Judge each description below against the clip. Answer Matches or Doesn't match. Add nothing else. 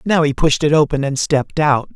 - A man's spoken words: Matches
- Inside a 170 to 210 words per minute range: Doesn't match